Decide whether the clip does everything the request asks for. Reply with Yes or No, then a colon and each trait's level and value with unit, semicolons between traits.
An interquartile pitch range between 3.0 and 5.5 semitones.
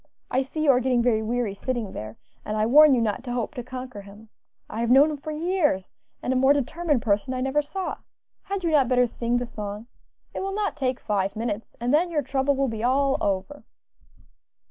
Yes: average, 4.4 semitones